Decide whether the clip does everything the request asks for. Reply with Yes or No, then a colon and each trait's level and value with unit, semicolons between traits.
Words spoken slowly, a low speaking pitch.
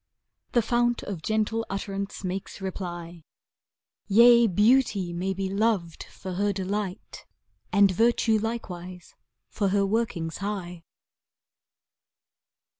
No: slow, 110 wpm; high, 200 Hz